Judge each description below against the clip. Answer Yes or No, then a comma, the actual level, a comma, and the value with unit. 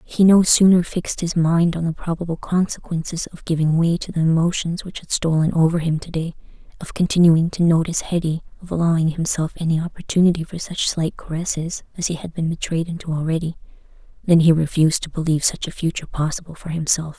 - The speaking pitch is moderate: Yes, medium, 165 Hz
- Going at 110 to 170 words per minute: No, average, 185 wpm